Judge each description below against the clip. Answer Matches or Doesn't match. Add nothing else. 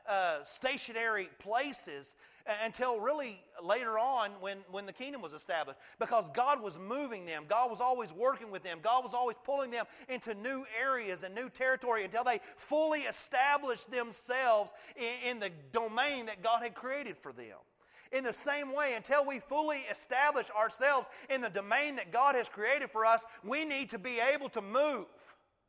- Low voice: Doesn't match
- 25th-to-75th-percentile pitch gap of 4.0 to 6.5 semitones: Doesn't match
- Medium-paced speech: Matches